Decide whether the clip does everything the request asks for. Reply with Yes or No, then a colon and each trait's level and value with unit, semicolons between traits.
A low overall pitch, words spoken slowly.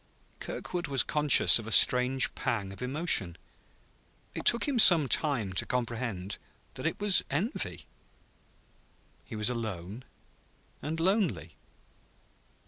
Yes: low, 125 Hz; slow, 120 wpm